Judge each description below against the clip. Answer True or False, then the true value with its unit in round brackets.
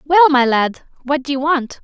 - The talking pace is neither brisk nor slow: False (230 wpm)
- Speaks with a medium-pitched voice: False (280 Hz)